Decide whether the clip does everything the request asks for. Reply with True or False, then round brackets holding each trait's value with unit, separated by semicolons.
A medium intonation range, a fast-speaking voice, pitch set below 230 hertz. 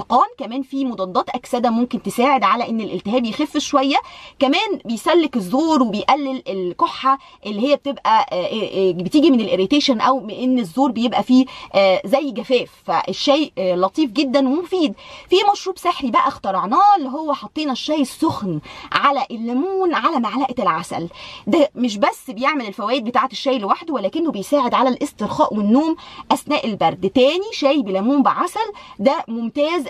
False (3.8 semitones; 145 wpm; 265 Hz)